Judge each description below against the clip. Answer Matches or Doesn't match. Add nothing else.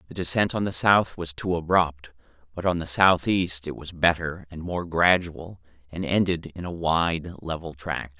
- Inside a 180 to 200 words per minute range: Matches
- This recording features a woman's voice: Doesn't match